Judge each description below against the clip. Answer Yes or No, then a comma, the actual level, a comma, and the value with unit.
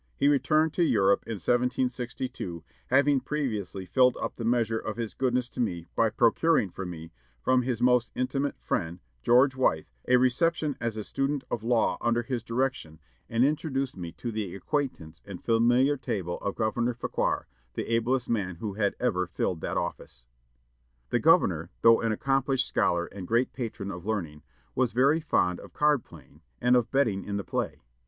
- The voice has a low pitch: Yes, low, 120 Hz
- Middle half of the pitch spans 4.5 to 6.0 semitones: Yes, average, 4.9 semitones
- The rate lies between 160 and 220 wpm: Yes, average, 175 wpm